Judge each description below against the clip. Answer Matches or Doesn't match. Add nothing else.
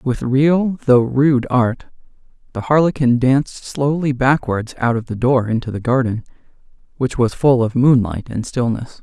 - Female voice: Doesn't match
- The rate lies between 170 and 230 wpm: Doesn't match